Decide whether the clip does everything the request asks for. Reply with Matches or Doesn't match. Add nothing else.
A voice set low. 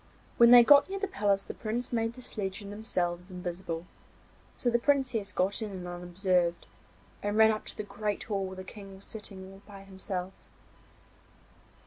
Doesn't match